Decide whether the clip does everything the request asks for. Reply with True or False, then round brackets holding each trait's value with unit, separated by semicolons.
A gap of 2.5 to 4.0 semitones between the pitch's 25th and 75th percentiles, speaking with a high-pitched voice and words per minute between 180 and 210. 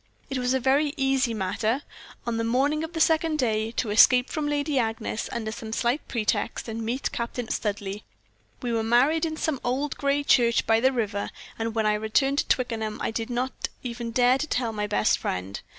True (3.5 semitones; 240 Hz; 200 wpm)